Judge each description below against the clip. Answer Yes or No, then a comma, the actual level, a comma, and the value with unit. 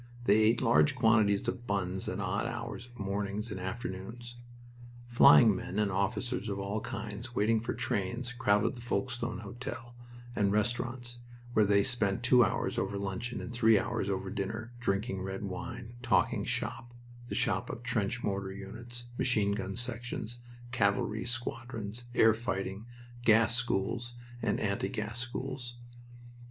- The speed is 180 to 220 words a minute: No, average, 145 wpm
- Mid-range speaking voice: No, low, 110 Hz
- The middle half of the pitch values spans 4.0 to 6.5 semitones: No, average, 3.2 semitones